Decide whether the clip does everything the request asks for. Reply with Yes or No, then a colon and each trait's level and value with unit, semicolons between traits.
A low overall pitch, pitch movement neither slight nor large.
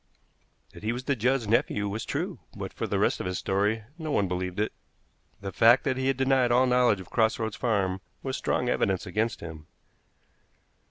Yes: low, 110 Hz; average, 4.4 semitones